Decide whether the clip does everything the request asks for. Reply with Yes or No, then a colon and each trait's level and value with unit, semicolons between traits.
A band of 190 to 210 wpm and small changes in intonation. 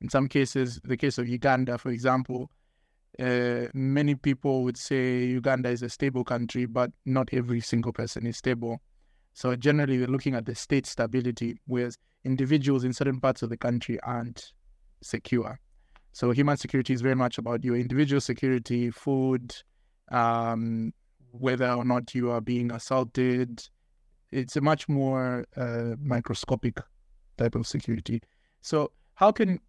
No: average, 150 wpm; narrow, 1.9 semitones